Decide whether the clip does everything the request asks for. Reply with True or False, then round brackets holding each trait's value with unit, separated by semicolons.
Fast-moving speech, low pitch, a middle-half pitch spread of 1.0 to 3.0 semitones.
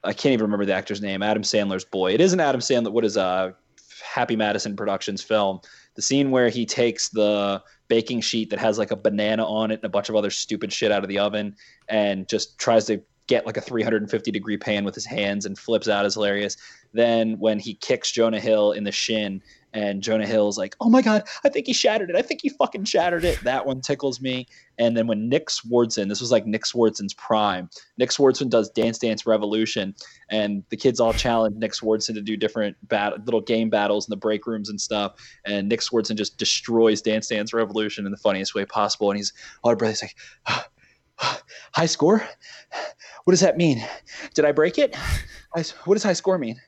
True (215 wpm; 110 Hz; 2.5 semitones)